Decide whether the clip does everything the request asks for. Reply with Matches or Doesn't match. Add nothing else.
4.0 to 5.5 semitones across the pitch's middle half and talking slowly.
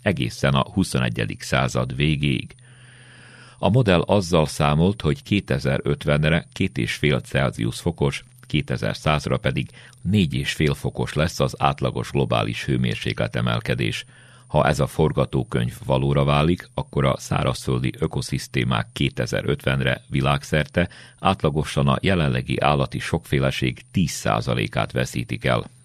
Matches